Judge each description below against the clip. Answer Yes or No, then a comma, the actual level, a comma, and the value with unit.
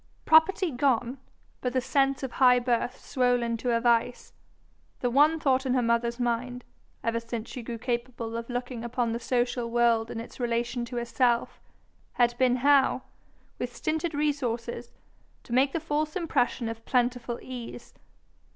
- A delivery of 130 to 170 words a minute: Yes, average, 160 wpm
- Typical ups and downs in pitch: No, narrow, 1.9 semitones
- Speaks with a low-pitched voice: No, high, 245 Hz